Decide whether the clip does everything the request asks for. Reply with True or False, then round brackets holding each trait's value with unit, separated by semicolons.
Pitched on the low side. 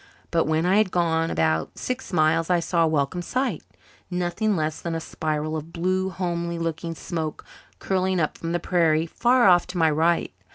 False (170 Hz)